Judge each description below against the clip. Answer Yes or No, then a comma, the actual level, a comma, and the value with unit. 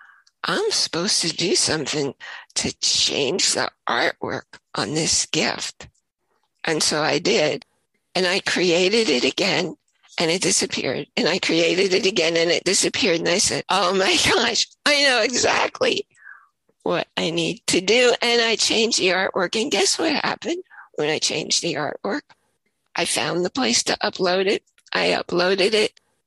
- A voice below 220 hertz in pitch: No, high, 225 Hz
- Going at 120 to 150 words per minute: No, average, 160 wpm